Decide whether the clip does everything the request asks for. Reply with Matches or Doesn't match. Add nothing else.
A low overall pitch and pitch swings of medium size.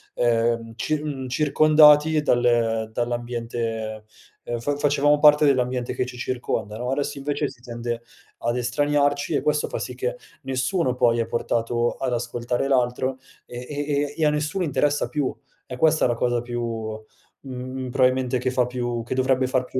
Matches